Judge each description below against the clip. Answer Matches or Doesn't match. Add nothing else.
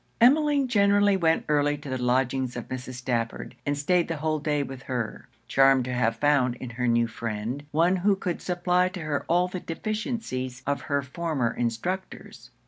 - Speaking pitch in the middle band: Matches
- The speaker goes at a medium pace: Matches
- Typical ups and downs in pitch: Doesn't match